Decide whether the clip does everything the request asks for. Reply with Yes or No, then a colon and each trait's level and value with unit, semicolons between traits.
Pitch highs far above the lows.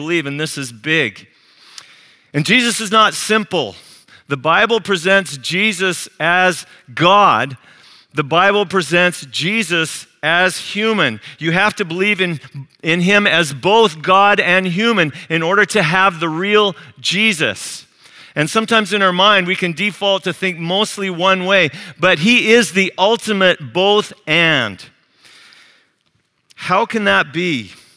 No: average, 4.0 semitones